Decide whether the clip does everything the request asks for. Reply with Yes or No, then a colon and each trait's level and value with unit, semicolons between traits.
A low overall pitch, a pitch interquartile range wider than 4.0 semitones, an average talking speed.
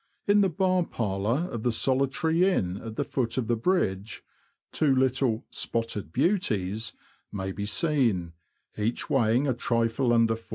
Yes: low, 120 Hz; average, 4.6 semitones; average, 155 wpm